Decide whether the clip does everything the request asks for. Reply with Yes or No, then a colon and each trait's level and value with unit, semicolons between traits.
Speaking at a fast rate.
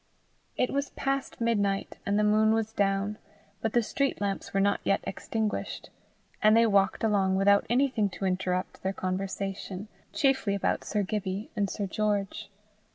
No: average, 160 wpm